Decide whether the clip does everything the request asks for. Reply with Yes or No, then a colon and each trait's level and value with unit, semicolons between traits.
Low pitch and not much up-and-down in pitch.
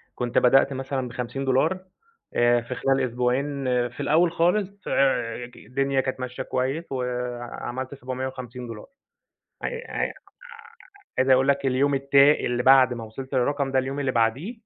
Yes: low, 130 Hz; narrow, 2.0 semitones